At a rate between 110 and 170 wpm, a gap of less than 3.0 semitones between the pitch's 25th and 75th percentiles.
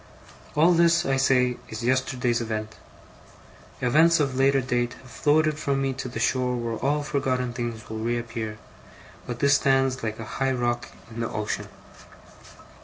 Yes: average, 160 wpm; narrow, 2.5 semitones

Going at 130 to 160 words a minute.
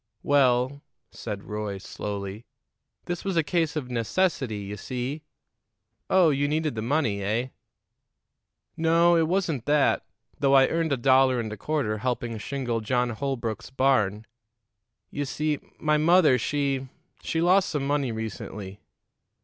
Yes: average, 140 wpm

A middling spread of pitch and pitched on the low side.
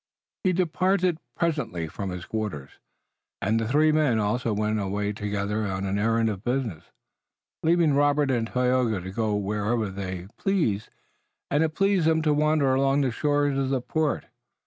No: wide, 6.6 semitones; low, 120 Hz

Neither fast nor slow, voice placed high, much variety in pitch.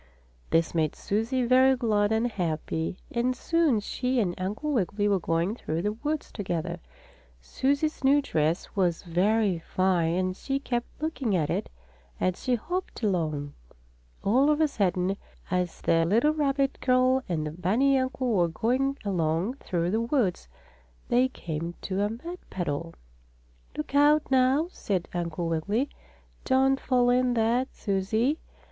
Yes: average, 150 wpm; high, 215 Hz; wide, 6.9 semitones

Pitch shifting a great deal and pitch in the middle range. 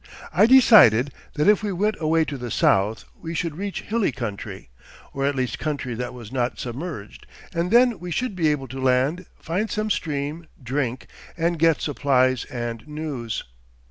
Yes: wide, 5.8 semitones; medium, 150 Hz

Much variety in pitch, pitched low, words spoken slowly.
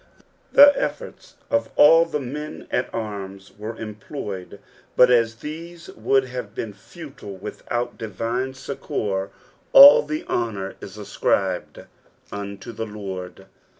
Yes: wide, 5.7 semitones; low, 115 Hz; slow, 120 wpm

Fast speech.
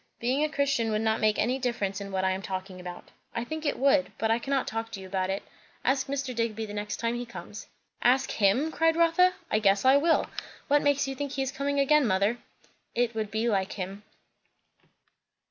Yes: fast, 215 wpm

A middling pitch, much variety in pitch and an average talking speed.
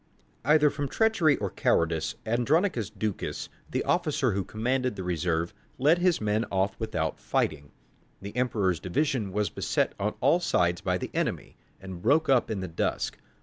No: low, 110 Hz; wide, 7.2 semitones; average, 160 wpm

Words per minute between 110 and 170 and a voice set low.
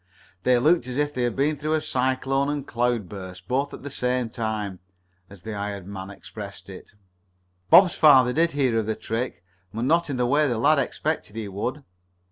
No: average, 200 wpm; low, 125 Hz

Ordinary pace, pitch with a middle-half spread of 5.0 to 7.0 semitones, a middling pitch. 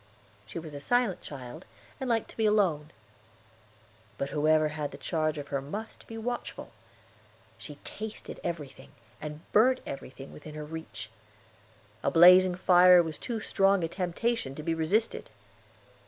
Yes: average, 150 wpm; wide, 5.6 semitones; medium, 165 Hz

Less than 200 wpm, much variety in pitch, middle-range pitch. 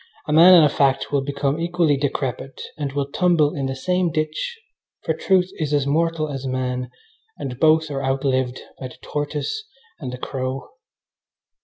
No: average, 170 wpm; average, 3.0 semitones; medium, 145 Hz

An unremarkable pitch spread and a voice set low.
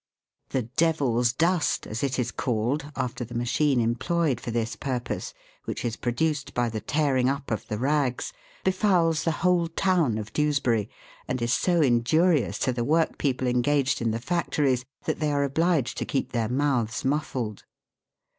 Yes: average, 4.4 semitones; low, 130 Hz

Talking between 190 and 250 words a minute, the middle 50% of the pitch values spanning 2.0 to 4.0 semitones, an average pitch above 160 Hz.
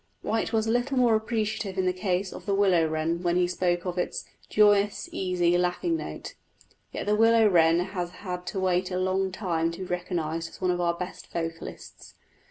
Yes: average, 200 wpm; average, 2.9 semitones; medium, 185 Hz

